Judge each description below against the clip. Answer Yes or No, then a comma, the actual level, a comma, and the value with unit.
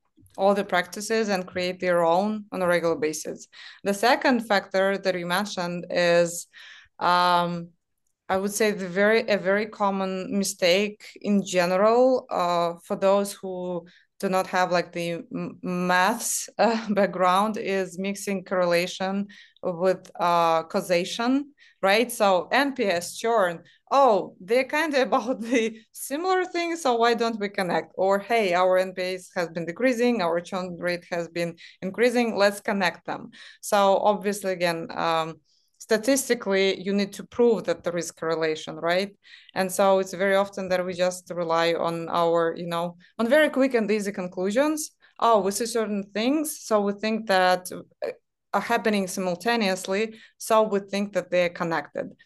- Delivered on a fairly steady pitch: No, average, 3.7 semitones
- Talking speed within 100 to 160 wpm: Yes, average, 155 wpm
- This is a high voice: Yes, high, 195 Hz